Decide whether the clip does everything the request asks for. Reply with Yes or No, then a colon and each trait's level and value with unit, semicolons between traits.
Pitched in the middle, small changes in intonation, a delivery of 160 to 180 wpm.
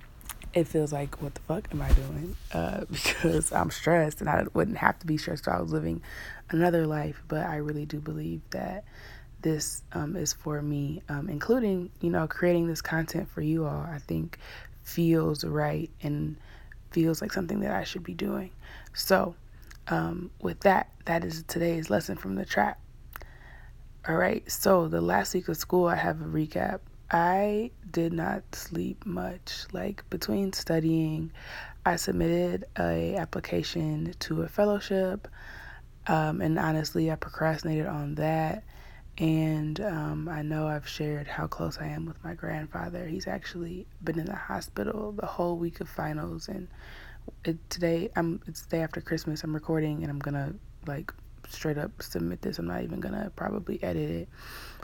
Yes: medium, 160 Hz; narrow, 2.2 semitones; average, 170 wpm